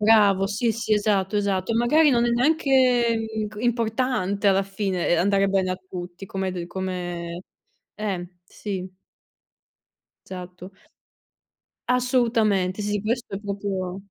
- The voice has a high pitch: Yes, high, 200 Hz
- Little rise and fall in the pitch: No, average, 3.5 semitones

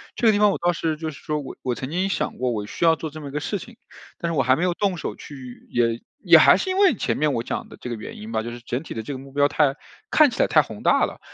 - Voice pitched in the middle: Yes, medium, 150 Hz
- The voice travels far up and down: Yes, wide, 5.8 semitones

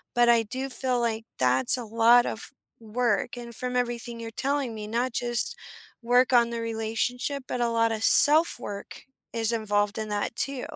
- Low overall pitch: No, high, 235 Hz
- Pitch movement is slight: Yes, narrow, 1.9 semitones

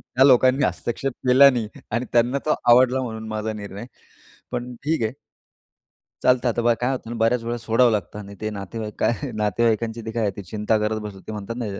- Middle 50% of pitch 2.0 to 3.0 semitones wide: Yes, narrow, 2.5 semitones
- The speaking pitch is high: No, low, 115 Hz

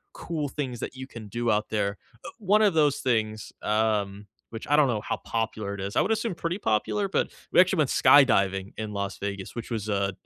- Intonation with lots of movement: Yes, wide, 6.3 semitones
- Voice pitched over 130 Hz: No, low, 110 Hz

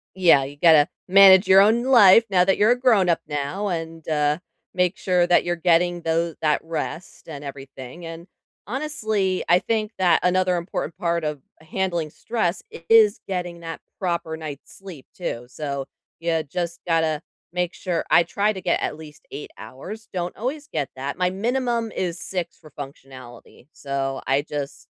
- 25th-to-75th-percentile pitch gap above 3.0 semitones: Yes, average, 3.9 semitones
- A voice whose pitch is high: No, medium, 170 Hz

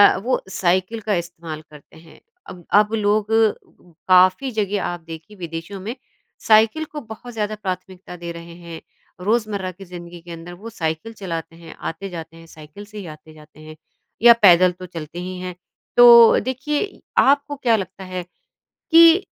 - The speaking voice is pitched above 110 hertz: Yes, medium, 185 Hz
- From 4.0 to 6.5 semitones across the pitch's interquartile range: Yes, average, 4.4 semitones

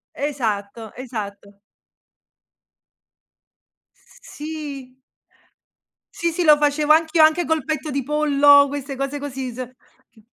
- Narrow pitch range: No, average, 3.1 semitones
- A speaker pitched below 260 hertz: No, very high, 285 Hz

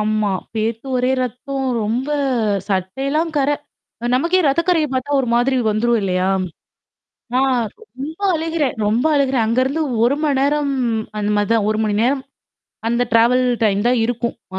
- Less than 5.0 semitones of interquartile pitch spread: Yes, average, 3.9 semitones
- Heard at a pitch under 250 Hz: No, very high, 255 Hz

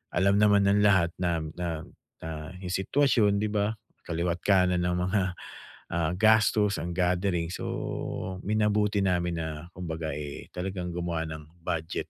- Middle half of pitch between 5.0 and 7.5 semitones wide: No, average, 3.2 semitones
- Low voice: Yes, very low, 90 Hz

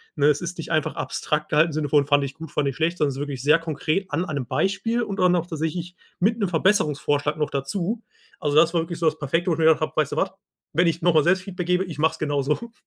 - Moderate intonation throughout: Yes, average, 3.1 semitones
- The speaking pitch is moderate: Yes, medium, 160 Hz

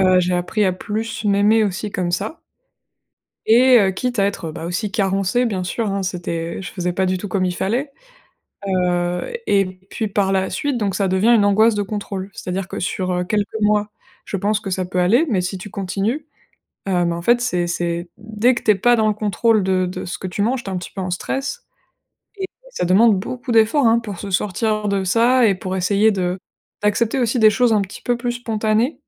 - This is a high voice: Yes, high, 200 Hz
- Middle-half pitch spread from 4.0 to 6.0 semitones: No, average, 3.4 semitones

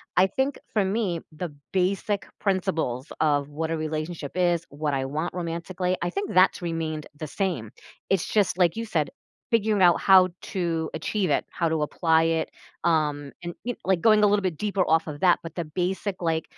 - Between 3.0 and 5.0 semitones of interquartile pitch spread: Yes, average, 3.3 semitones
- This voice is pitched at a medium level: Yes, medium, 175 Hz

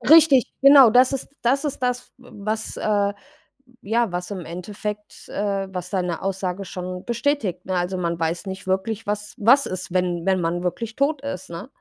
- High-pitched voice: Yes, high, 200 Hz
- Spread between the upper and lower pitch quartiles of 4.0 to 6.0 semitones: Yes, average, 4.7 semitones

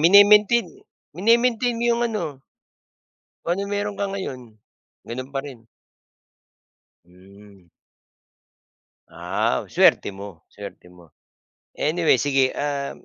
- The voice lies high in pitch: No, medium, 155 Hz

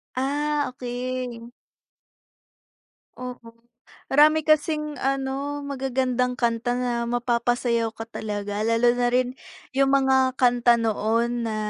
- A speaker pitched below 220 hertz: No, very high, 250 Hz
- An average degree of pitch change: No, narrow, 2.3 semitones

